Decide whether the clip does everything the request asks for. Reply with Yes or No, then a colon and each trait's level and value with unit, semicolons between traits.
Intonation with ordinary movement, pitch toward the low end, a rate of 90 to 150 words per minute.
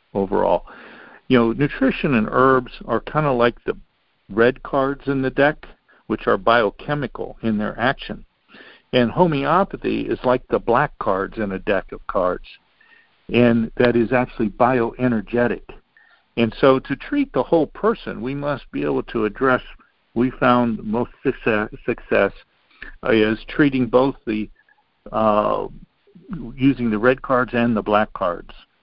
Yes: average, 3.0 semitones; low, 125 Hz; average, 145 wpm